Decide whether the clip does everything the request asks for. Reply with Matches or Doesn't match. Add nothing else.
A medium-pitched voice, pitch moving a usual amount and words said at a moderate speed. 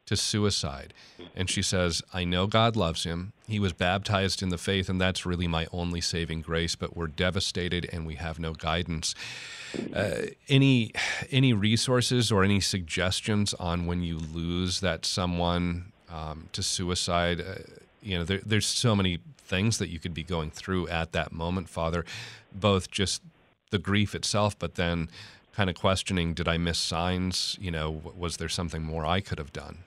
Doesn't match